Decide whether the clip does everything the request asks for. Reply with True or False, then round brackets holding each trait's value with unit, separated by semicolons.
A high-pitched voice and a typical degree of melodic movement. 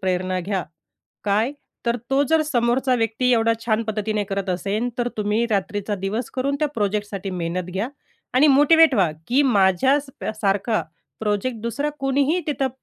True (220 Hz; 4.9 semitones)